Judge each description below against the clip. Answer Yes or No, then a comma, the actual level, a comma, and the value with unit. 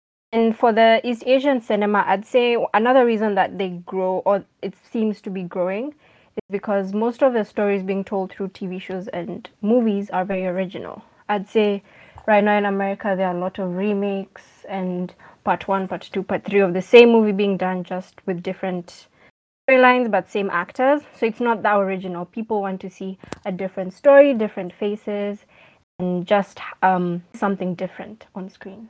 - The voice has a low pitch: No, high, 200 Hz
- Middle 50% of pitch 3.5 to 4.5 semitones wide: No, narrow, 2.5 semitones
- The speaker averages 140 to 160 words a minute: No, average, 185 wpm